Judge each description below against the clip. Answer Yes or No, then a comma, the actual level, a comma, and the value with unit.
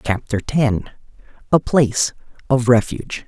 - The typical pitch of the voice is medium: No, low, 120 Hz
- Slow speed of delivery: Yes, slow, 110 wpm